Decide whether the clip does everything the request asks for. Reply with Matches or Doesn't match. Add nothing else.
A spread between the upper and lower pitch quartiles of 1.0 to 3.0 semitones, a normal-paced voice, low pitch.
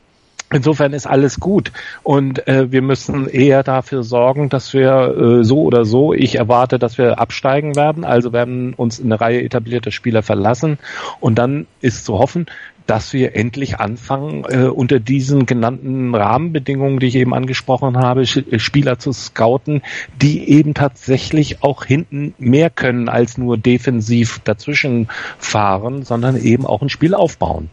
Matches